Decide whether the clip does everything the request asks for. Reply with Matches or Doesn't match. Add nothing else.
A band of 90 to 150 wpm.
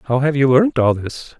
Doesn't match